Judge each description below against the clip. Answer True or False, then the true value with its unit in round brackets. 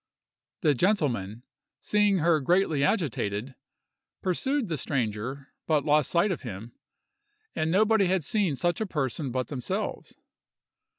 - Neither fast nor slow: False (125 wpm)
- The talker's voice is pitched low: False (155 Hz)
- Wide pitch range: True (6.5 semitones)